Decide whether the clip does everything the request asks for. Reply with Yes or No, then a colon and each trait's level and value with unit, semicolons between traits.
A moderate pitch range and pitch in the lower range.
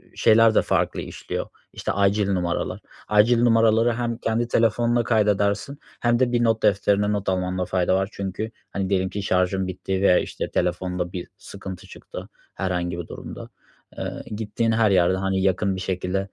Yes: average, 3.3 semitones; low, 100 Hz